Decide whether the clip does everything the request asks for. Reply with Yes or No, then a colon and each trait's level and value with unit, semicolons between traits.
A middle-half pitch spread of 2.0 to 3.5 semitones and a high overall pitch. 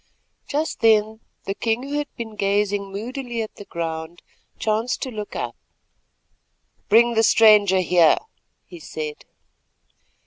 Yes: average, 2.9 semitones; high, 215 Hz